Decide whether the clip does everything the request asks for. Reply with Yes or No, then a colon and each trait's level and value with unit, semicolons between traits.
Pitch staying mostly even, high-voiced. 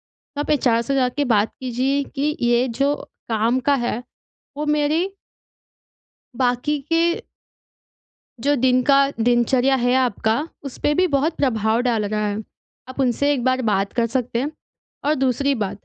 No: average, 3.3 semitones; very high, 255 Hz